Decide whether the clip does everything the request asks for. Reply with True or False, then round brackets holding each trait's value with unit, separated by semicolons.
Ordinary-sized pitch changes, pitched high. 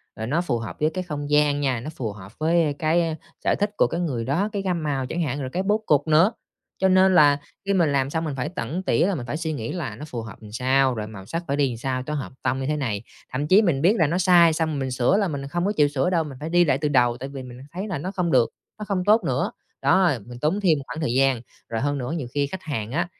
False (4.9 semitones; 150 Hz)